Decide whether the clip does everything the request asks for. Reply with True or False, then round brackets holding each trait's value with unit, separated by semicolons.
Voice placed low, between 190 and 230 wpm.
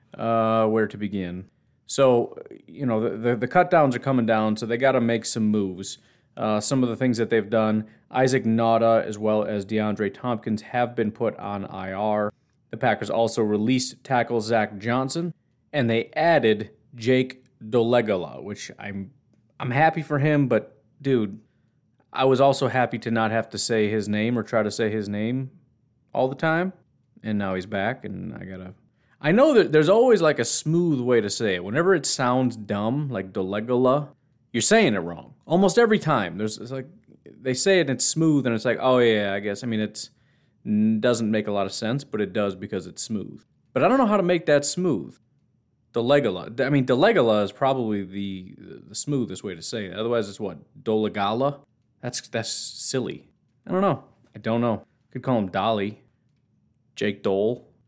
True (115 Hz; 195 wpm)